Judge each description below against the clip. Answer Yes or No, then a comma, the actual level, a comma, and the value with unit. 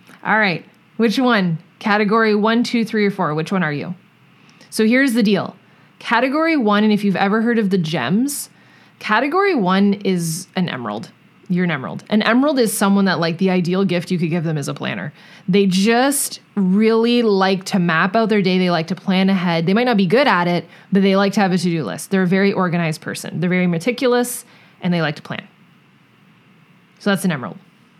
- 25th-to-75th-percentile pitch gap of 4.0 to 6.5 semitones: No, average, 3.4 semitones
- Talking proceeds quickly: Yes, fast, 210 wpm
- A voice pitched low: No, high, 195 Hz